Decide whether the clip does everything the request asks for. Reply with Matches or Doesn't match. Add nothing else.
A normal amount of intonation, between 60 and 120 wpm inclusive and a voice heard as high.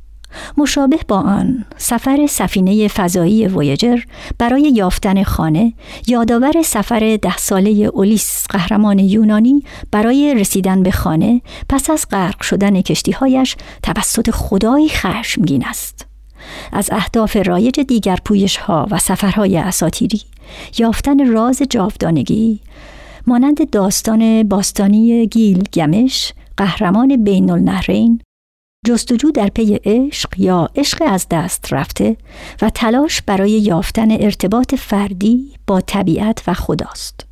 Matches